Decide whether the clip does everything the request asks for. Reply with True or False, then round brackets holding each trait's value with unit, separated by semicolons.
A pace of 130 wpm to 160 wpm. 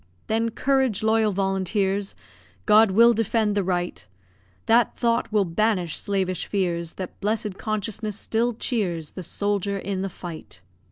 True (135 wpm)